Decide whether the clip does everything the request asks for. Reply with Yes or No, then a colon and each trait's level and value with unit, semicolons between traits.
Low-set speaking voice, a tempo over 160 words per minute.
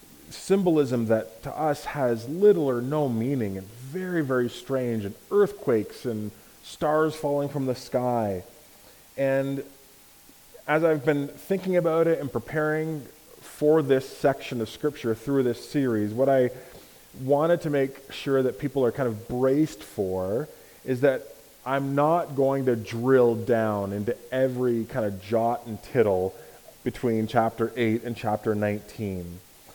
No: low, 130 Hz; average, 145 wpm